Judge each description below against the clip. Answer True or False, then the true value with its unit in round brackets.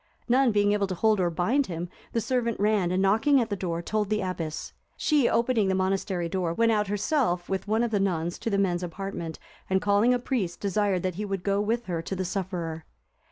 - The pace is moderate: False (225 wpm)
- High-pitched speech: True (195 Hz)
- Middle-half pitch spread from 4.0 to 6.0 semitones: False (3.5 semitones)